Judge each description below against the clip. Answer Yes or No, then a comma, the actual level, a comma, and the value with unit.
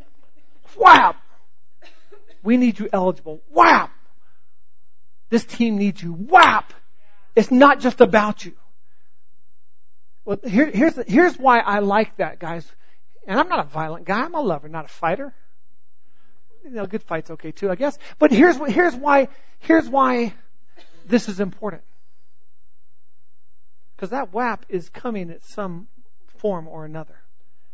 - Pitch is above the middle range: Yes, high, 200 Hz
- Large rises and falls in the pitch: Yes, wide, 8.1 semitones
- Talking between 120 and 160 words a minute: Yes, average, 140 wpm